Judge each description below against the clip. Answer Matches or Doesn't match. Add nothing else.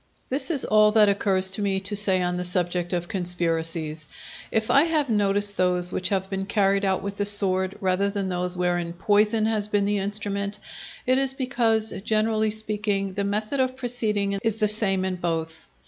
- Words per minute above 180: Matches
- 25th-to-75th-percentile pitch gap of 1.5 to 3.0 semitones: Matches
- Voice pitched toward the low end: Doesn't match